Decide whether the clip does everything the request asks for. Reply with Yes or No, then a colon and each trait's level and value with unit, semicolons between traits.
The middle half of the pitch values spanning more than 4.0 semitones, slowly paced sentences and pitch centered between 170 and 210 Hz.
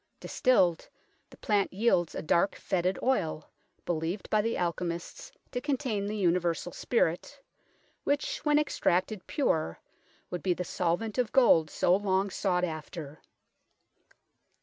Yes: average, 4.7 semitones; slow, 130 wpm; medium, 185 Hz